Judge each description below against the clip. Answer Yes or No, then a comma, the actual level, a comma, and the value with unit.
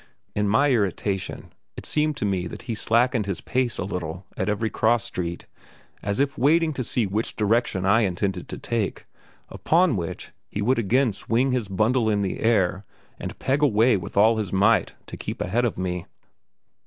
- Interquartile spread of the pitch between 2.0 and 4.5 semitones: Yes, average, 4.1 semitones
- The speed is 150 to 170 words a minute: No, average, 185 wpm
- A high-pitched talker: No, low, 110 Hz